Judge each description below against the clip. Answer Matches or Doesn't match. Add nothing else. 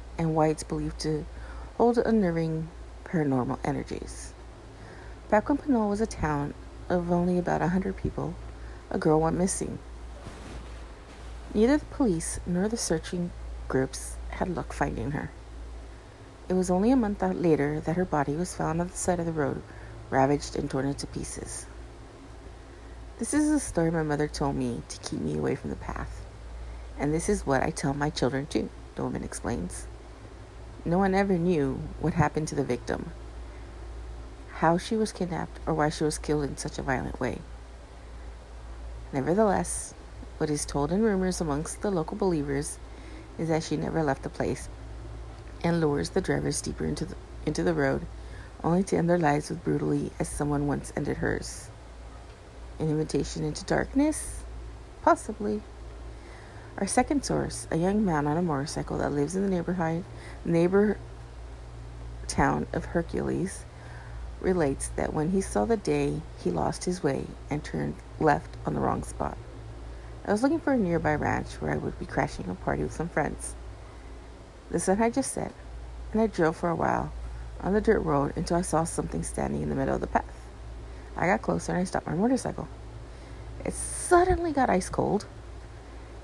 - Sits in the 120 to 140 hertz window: Doesn't match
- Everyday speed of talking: Matches